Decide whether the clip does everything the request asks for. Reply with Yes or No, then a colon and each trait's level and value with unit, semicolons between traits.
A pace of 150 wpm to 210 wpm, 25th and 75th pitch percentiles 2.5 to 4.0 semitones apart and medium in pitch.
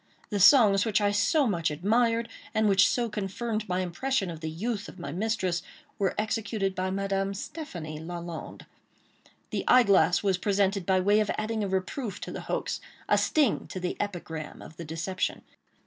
No: average, 170 wpm; average, 3.3 semitones; high, 195 Hz